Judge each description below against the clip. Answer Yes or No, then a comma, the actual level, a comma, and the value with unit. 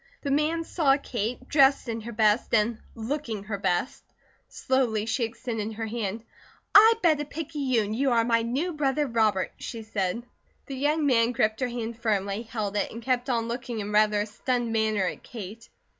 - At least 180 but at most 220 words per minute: Yes, average, 185 wpm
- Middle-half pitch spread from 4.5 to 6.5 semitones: No, average, 3.6 semitones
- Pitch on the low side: No, high, 230 Hz